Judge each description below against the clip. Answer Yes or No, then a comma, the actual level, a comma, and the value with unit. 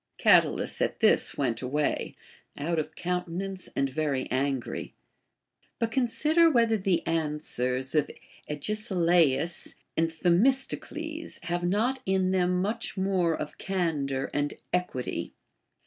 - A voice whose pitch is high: No, medium, 175 Hz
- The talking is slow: Yes, slow, 115 wpm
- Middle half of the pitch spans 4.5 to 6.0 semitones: Yes, average, 4.9 semitones